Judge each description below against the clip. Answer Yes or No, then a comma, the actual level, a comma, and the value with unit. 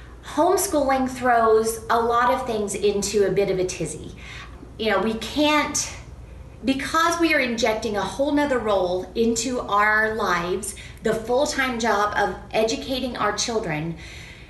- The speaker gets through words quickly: No, average, 145 wpm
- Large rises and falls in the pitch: No, average, 4.4 semitones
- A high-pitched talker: Yes, high, 220 Hz